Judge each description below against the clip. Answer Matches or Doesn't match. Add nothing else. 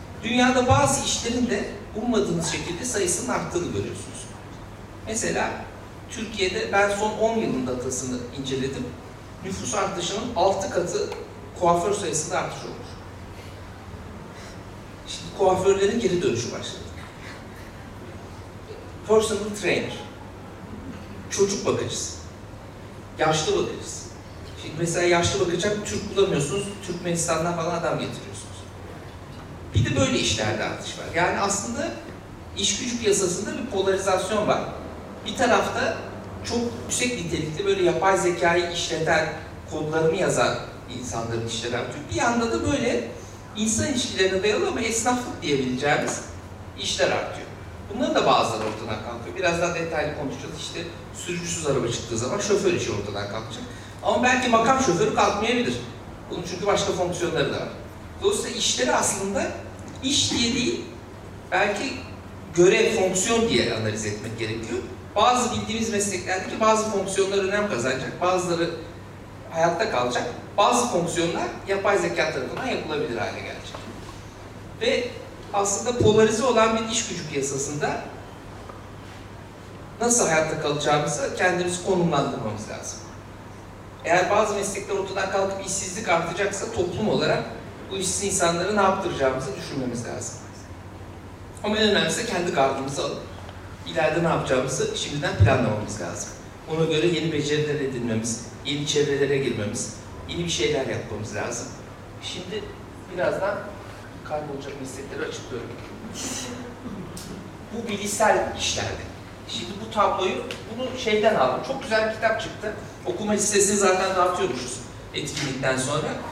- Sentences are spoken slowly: Doesn't match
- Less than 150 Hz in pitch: Matches